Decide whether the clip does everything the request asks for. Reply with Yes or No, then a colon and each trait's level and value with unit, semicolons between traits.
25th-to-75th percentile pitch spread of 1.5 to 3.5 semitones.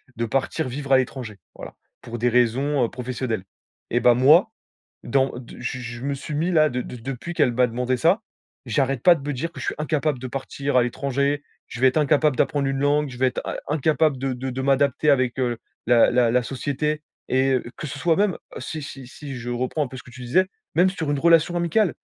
Yes: average, 3.2 semitones